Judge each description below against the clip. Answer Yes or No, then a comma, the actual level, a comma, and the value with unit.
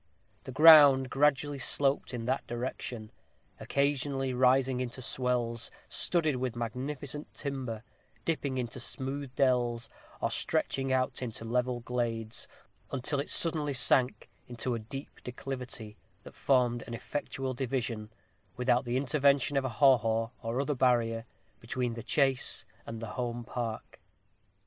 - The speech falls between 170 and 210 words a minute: No, slow, 135 wpm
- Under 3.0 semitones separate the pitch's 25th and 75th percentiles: Yes, narrow, 2.4 semitones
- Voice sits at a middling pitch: No, low, 125 Hz